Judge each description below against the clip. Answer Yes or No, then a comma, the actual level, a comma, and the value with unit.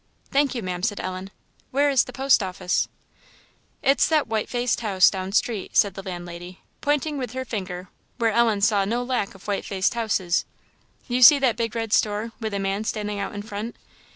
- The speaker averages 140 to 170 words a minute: No, average, 195 wpm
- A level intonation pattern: No, average, 3.9 semitones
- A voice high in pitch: Yes, high, 215 Hz